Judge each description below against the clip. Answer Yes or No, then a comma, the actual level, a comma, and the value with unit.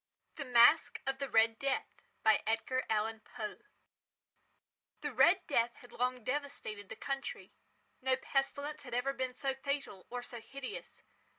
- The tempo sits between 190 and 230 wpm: No, average, 150 wpm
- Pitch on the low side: No, very high, 255 Hz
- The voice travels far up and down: No, average, 3.4 semitones